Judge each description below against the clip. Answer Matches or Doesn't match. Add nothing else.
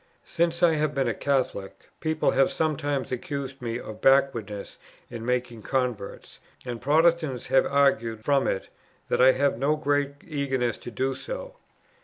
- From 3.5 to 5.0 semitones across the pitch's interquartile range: Doesn't match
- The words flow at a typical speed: Matches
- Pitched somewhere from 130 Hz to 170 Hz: Matches